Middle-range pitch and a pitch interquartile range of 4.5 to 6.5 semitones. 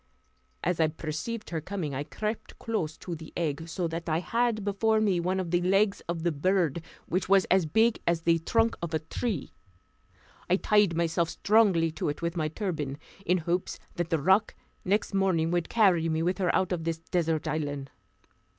No: medium, 175 Hz; average, 3.4 semitones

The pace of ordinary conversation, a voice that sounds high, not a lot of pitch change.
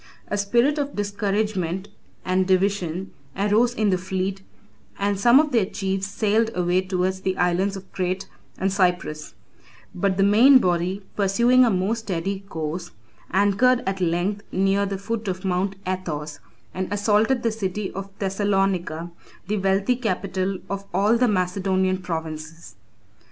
Yes: average, 145 wpm; high, 195 Hz; narrow, 2.0 semitones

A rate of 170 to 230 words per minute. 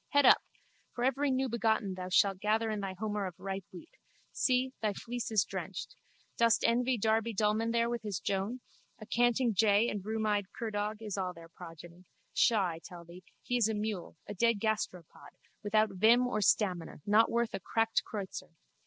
Yes: average, 180 wpm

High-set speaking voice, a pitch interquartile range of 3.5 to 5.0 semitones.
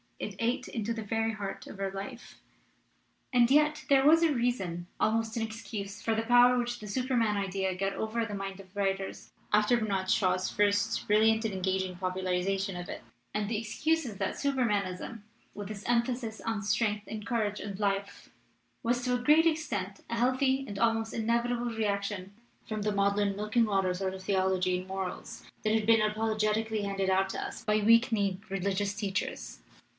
No: high, 210 Hz; average, 3.0 semitones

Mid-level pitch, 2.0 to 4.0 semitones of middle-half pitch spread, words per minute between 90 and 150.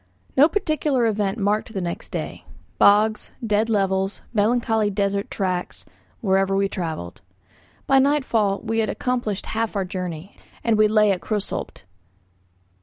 No: high, 210 Hz; narrow, 2.6 semitones; slow, 135 wpm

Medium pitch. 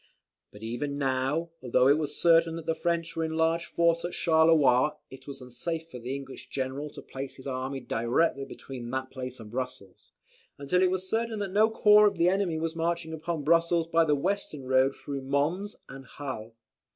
Yes: medium, 150 Hz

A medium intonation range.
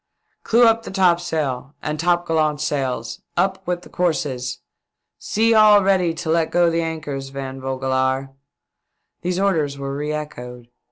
Yes: average, 4.7 semitones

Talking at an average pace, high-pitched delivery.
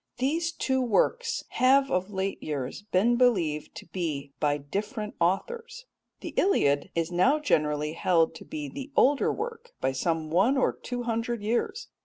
Yes: average, 160 wpm; high, 215 Hz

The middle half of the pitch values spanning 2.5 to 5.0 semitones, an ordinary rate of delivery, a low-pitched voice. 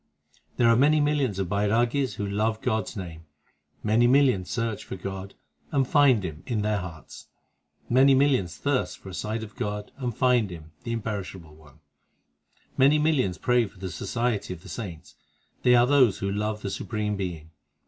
Yes: average, 4.5 semitones; average, 180 wpm; low, 110 Hz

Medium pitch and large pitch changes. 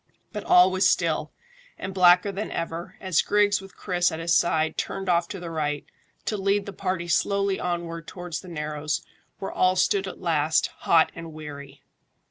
No: medium, 175 Hz; average, 3.1 semitones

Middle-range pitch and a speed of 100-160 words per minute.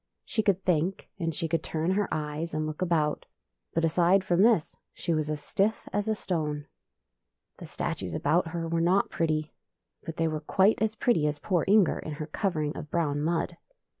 No: medium, 165 Hz; average, 195 wpm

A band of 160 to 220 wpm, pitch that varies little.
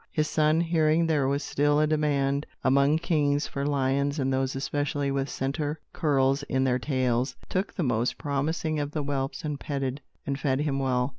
Yes: average, 180 wpm; narrow, 2.1 semitones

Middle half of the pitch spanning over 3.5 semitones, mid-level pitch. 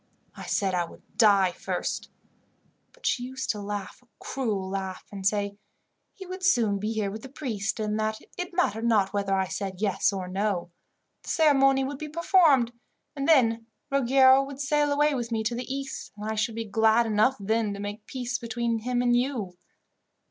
No: average, 4.7 semitones; high, 225 Hz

